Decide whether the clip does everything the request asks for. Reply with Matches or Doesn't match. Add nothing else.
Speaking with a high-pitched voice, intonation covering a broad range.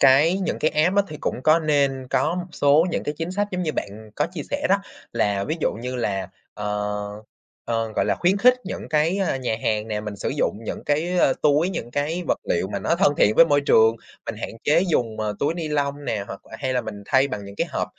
Doesn't match